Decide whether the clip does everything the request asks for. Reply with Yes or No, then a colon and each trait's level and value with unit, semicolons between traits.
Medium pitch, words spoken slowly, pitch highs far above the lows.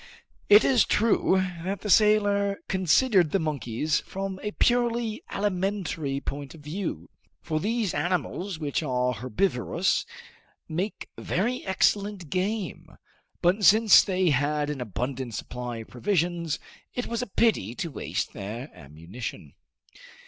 Yes: medium, 180 Hz; slow, 125 wpm; wide, 6.8 semitones